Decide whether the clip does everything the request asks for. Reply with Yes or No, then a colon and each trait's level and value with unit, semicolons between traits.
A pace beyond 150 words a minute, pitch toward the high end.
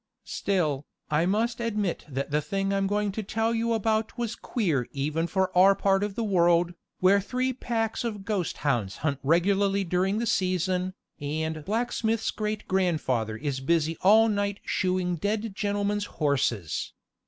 Yes: average, 160 wpm; high, 195 Hz